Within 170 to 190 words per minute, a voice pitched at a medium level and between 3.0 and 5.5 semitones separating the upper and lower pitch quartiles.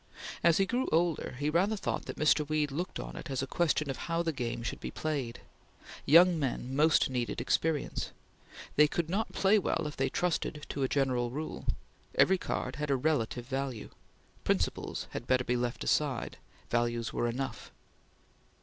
Yes: average, 175 wpm; medium, 145 Hz; average, 4.4 semitones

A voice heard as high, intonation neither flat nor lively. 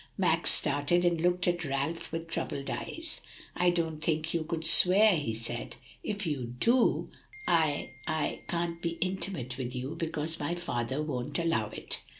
No: medium, 165 Hz; average, 3.5 semitones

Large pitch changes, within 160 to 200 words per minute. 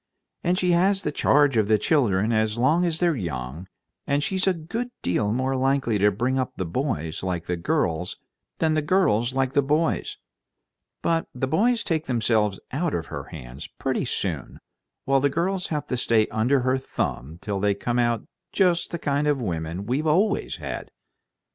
Yes: wide, 7.3 semitones; average, 180 wpm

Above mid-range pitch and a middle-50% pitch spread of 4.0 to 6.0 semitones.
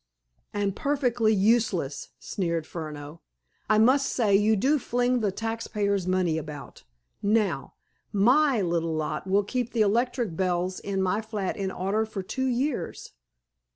Yes: high, 205 Hz; average, 4.3 semitones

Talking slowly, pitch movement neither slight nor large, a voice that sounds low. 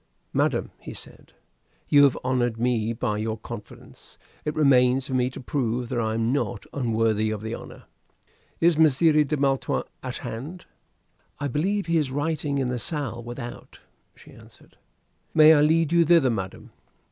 No: average, 165 wpm; average, 4.5 semitones; low, 130 Hz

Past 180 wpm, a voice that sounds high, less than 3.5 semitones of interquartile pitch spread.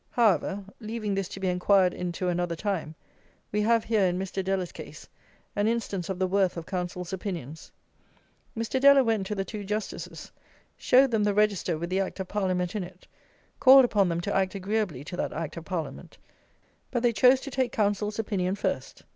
Yes: average, 190 wpm; high, 195 Hz; average, 3.1 semitones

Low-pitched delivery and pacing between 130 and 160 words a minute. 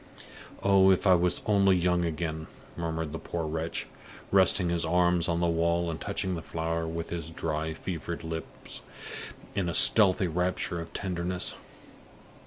Yes: very low, 85 Hz; average, 155 wpm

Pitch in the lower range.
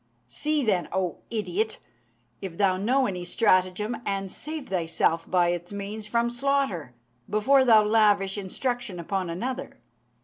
No: high, 205 Hz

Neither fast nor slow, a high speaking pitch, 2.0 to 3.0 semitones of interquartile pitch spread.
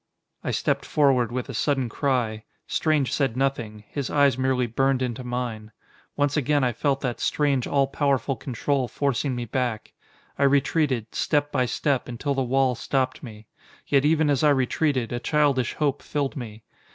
No: average, 170 wpm; low, 135 Hz; average, 2.7 semitones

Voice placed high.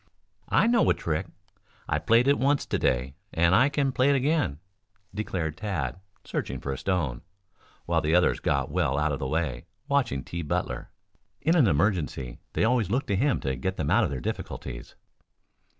No: very low, 85 Hz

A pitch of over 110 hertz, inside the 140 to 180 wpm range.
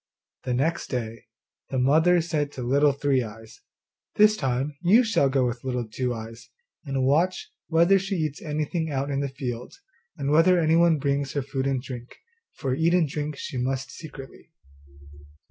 Yes: medium, 140 Hz; average, 170 wpm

